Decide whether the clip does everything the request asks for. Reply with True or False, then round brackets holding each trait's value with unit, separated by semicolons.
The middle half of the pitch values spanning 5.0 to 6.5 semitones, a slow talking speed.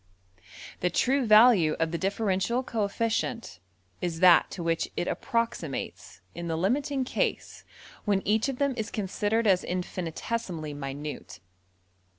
True (5.5 semitones; 130 wpm)